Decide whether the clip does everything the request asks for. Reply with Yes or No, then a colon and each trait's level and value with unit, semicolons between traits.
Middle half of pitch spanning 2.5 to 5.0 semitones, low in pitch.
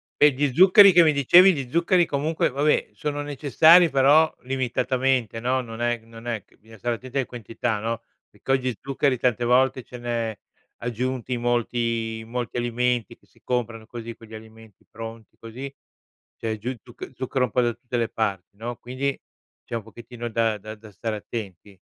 Yes: average, 2.8 semitones; low, 120 Hz